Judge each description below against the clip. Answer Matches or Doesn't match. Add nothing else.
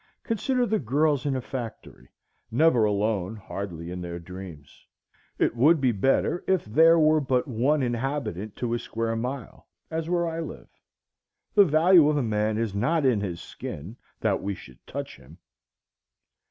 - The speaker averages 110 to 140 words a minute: Doesn't match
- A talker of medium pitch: Doesn't match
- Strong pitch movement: Matches